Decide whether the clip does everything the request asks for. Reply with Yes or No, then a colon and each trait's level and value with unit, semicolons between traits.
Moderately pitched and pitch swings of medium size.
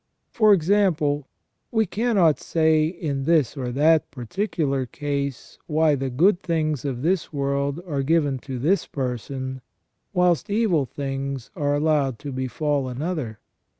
Yes: medium, 145 Hz; average, 3.6 semitones